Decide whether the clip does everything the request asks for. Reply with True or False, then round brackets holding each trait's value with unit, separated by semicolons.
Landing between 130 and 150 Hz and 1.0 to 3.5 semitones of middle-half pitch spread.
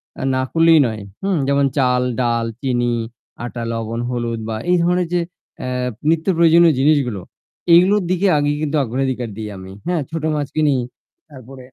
False (140 Hz; 5.3 semitones)